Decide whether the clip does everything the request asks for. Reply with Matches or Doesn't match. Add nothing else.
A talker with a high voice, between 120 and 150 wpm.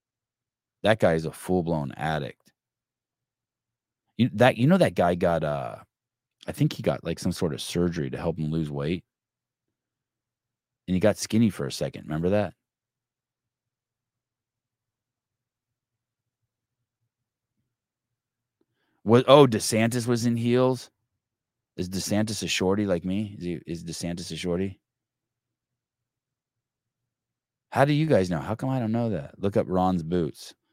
Doesn't match